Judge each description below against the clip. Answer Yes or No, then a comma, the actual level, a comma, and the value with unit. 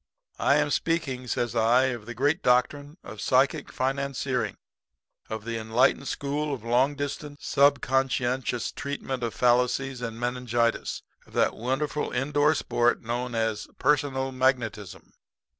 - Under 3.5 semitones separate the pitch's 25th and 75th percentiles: Yes, average, 2.8 semitones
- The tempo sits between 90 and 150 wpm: Yes, average, 140 wpm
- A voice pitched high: No, low, 130 Hz